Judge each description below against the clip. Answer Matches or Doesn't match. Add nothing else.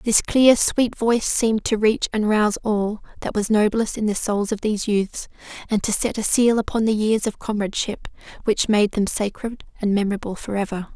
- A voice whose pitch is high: Matches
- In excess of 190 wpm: Matches